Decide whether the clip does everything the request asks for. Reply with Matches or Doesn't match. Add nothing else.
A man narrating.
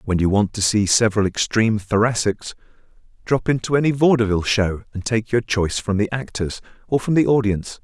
Matches